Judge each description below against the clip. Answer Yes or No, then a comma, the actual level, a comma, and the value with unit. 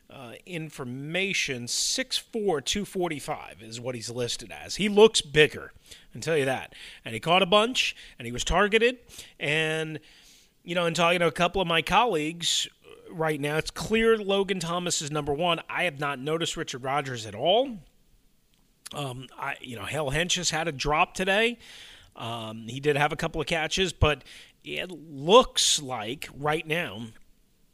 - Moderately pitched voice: Yes, medium, 160 Hz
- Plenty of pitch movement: No, average, 4.6 semitones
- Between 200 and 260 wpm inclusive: No, average, 175 wpm